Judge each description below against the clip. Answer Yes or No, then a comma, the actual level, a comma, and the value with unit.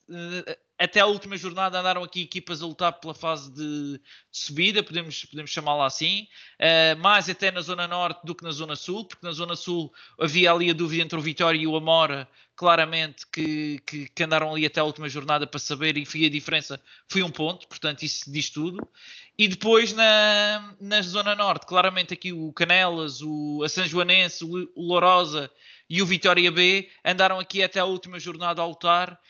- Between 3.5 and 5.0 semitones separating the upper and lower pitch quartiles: No, average, 2.8 semitones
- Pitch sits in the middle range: Yes, medium, 170 Hz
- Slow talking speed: No, fast, 185 wpm